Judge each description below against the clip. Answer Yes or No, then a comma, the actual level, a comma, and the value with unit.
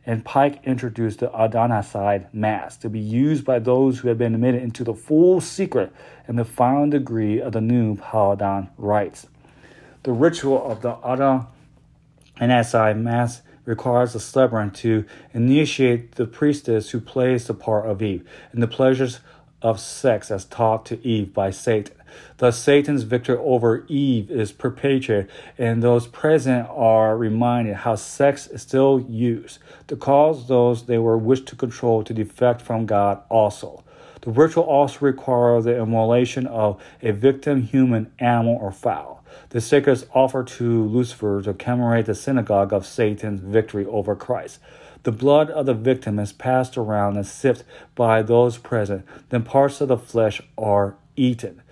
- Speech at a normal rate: Yes, average, 160 wpm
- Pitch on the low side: Yes, low, 120 Hz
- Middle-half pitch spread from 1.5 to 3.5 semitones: Yes, average, 3.0 semitones